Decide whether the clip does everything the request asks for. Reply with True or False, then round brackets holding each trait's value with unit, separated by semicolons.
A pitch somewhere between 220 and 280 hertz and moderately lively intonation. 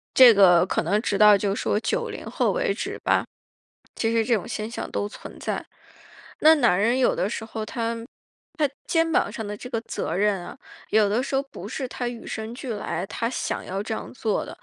True (225 Hz; 3.1 semitones)